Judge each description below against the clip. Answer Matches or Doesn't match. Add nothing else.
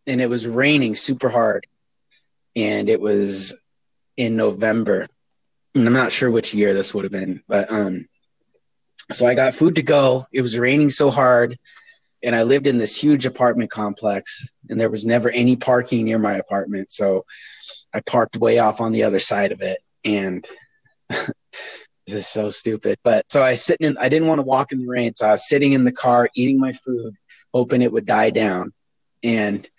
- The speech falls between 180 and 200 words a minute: Matches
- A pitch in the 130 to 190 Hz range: Doesn't match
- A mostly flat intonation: Doesn't match